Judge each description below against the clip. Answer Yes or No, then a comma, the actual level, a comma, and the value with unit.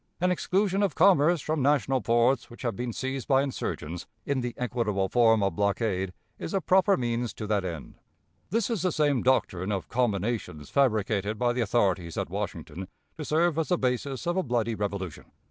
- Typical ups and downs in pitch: No, wide, 6.3 semitones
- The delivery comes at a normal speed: Yes, average, 185 wpm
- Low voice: Yes, low, 120 Hz